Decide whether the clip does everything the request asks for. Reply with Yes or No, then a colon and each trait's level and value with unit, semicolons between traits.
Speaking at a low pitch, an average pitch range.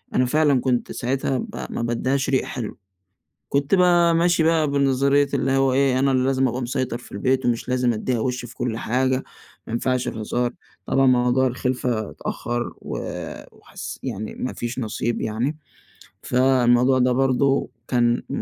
No: low, 130 Hz; narrow, 1.9 semitones